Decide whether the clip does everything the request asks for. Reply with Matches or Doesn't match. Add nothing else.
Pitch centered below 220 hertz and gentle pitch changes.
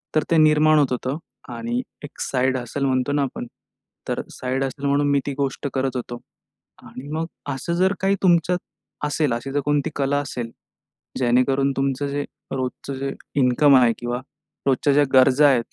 Matches